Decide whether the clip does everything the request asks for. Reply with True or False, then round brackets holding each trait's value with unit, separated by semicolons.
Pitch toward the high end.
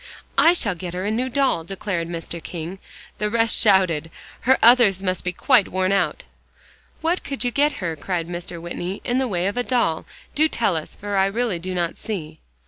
True (195 Hz)